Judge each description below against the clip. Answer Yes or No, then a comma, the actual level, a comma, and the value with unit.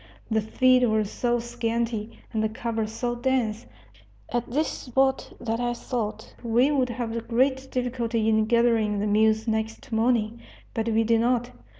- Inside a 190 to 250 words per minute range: No, average, 160 wpm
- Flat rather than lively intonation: Yes, narrow, 1.8 semitones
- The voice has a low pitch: No, high, 230 Hz